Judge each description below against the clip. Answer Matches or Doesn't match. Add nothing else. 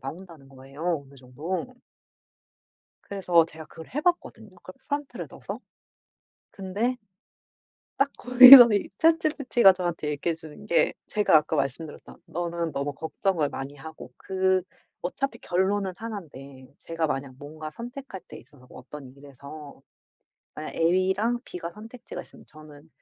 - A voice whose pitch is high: Doesn't match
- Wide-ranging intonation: Matches